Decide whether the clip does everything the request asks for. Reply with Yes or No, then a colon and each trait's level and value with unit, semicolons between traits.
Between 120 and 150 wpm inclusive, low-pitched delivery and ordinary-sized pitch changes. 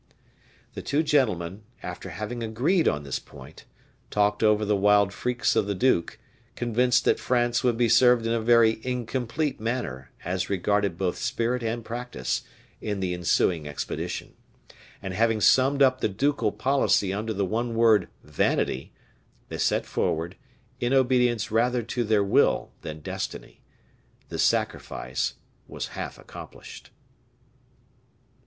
Yes: average, 140 wpm; low, 110 Hz; average, 3.8 semitones